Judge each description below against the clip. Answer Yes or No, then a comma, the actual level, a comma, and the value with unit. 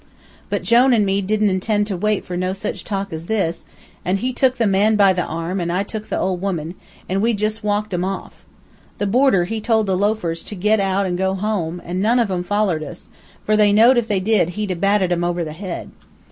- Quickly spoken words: Yes, fast, 240 wpm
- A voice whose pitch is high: Yes, high, 195 Hz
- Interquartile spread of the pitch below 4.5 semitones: Yes, average, 3.0 semitones